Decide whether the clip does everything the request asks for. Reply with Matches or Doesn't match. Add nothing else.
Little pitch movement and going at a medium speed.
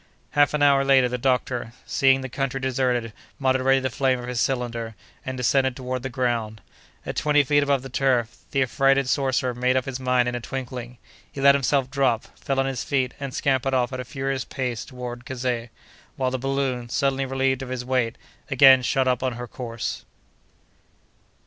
Matches